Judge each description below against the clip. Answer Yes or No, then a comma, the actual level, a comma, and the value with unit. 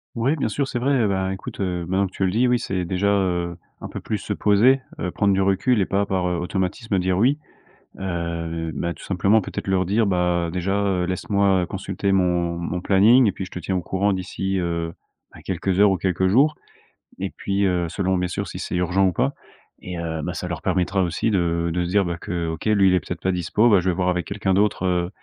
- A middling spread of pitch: No, narrow, 2.1 semitones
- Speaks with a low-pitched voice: Yes, very low, 95 Hz